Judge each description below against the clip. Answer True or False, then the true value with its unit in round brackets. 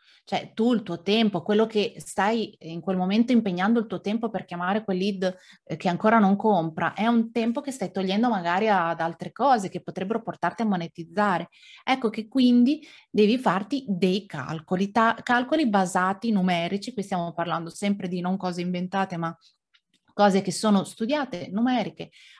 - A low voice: False (200 Hz)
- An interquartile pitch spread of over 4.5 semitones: False (4.1 semitones)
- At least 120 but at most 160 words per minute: False (170 wpm)